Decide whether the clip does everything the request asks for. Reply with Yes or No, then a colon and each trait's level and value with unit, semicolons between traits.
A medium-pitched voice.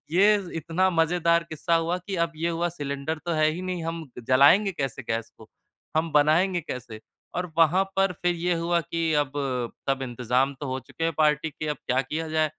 Yes: medium, 165 Hz